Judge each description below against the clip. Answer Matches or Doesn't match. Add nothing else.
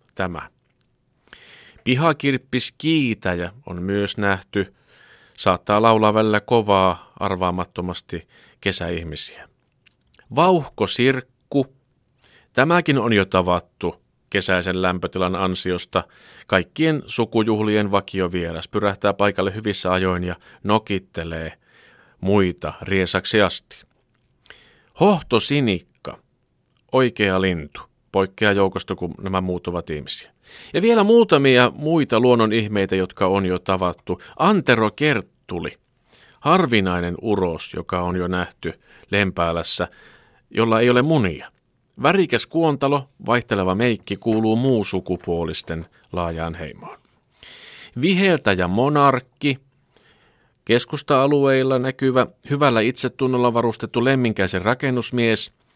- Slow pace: Matches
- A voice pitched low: Matches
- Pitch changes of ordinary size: Doesn't match